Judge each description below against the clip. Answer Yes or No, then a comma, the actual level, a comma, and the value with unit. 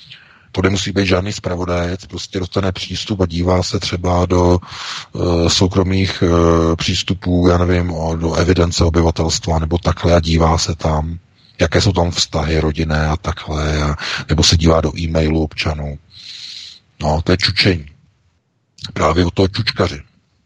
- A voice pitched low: Yes, very low, 90 Hz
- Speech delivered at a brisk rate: No, average, 145 wpm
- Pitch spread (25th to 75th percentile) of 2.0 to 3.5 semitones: Yes, narrow, 2.6 semitones